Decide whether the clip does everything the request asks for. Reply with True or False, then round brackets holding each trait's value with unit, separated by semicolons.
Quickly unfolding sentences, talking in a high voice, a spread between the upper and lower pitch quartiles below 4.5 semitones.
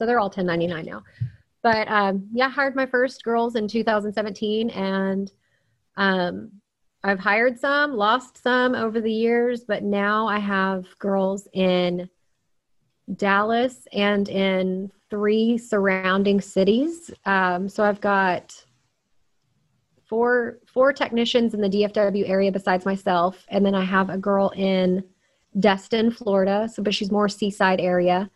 False (140 wpm; 200 Hz; 2.9 semitones)